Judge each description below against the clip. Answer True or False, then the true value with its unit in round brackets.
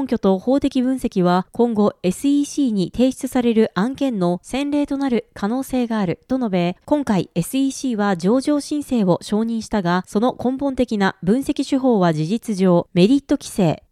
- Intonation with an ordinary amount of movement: False (5.8 semitones)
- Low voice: False (235 Hz)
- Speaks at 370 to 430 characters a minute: False (315 characters per minute)